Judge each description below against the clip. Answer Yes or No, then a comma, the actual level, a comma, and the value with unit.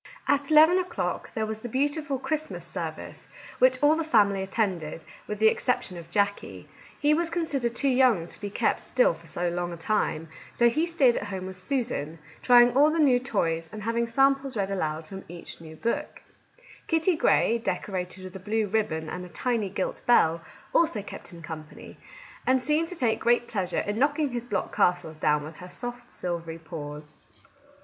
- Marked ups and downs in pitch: Yes, wide, 7.4 semitones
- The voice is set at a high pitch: Yes, high, 220 Hz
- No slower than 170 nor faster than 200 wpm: Yes, average, 190 wpm